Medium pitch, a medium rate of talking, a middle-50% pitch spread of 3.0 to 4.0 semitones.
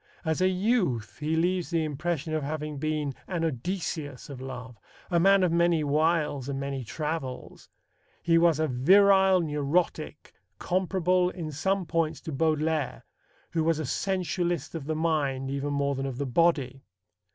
Yes: medium, 155 Hz; average, 160 wpm; average, 3.6 semitones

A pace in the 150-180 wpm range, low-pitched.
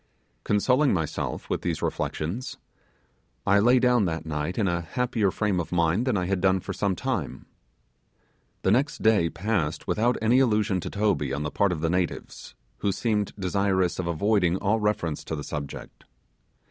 Yes: average, 170 wpm; low, 100 Hz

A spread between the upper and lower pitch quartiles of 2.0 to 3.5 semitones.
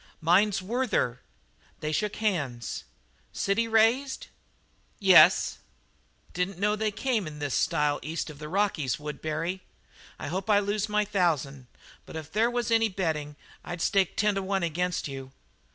No: wide, 5.6 semitones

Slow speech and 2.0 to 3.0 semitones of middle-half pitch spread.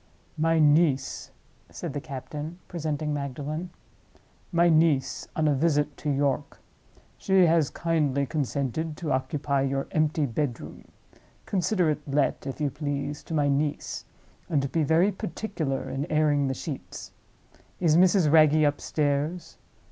Yes: slow, 130 wpm; narrow, 2.5 semitones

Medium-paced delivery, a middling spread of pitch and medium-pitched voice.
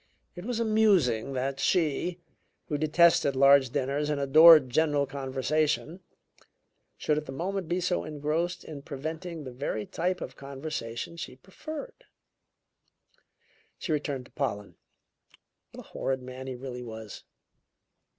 No: slow, 130 wpm; average, 4.2 semitones; medium, 145 Hz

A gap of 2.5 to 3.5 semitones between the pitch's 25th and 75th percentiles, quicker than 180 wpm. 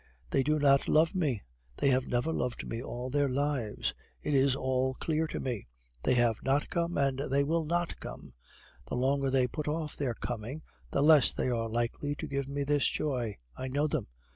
Yes: average, 2.8 semitones; average, 200 wpm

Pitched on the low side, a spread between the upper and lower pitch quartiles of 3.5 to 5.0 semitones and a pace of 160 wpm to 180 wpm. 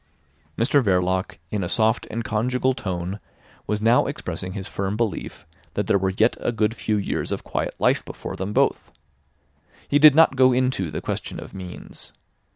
Yes: low, 105 Hz; average, 4.5 semitones; average, 175 wpm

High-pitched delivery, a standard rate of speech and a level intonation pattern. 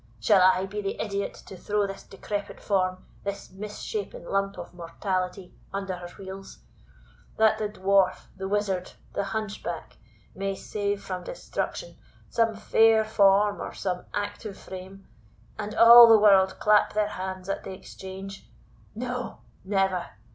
Yes: high, 195 Hz; average, 145 wpm; narrow, 1.8 semitones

